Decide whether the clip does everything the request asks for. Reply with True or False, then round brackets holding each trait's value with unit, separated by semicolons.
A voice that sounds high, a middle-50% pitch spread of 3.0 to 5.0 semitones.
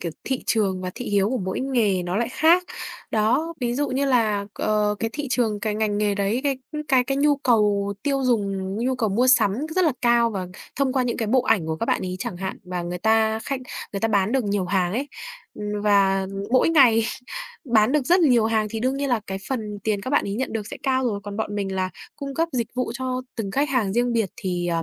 True (220 Hz; 4.3 semitones)